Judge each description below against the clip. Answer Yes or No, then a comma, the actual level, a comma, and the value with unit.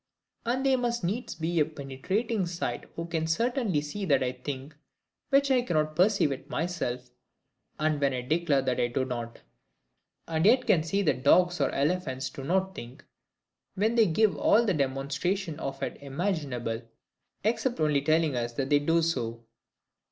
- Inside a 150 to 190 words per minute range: Yes, average, 170 wpm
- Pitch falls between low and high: Yes, medium, 160 Hz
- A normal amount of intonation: No, wide, 5.9 semitones